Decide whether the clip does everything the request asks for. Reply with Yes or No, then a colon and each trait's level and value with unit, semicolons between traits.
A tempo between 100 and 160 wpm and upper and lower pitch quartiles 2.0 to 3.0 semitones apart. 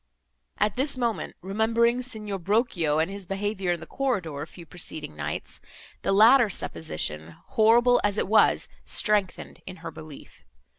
No: average, 150 wpm; average, 5.3 semitones